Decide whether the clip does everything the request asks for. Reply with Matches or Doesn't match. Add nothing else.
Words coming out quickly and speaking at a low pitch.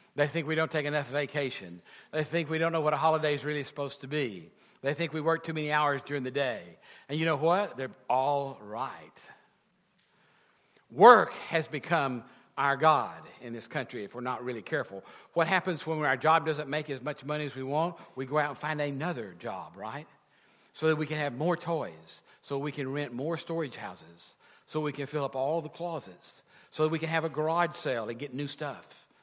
Doesn't match